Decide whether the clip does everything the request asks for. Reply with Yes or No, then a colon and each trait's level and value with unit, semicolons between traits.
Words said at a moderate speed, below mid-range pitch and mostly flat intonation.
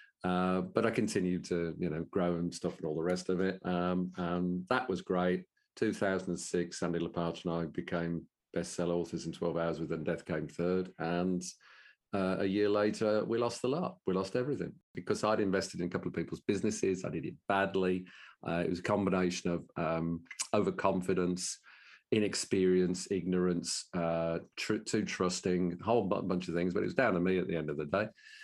Yes: average, 195 wpm; very low, 90 Hz; narrow, 1.6 semitones